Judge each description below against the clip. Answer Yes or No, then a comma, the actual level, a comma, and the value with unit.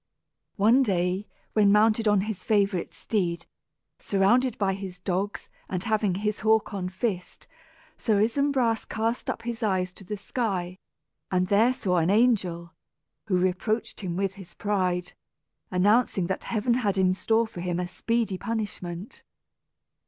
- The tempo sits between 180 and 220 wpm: No, average, 145 wpm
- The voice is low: No, high, 200 Hz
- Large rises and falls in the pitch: No, average, 3.3 semitones